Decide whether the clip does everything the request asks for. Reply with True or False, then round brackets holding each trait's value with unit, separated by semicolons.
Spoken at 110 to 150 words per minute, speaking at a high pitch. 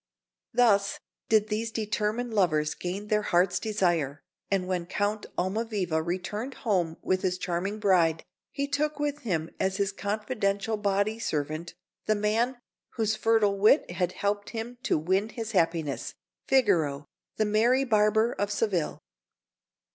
True (140 wpm; 205 Hz)